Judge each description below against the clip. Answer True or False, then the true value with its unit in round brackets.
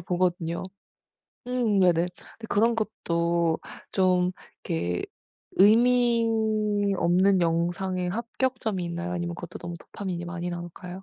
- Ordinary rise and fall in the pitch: True (3.1 semitones)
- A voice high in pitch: False (180 Hz)